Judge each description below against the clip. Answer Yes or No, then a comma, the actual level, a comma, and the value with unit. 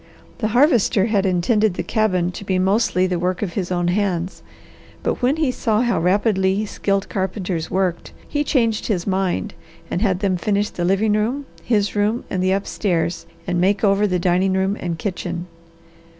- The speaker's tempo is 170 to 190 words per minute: Yes, average, 180 wpm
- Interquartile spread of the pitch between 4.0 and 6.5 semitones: No, average, 2.8 semitones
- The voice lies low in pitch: No, high, 195 Hz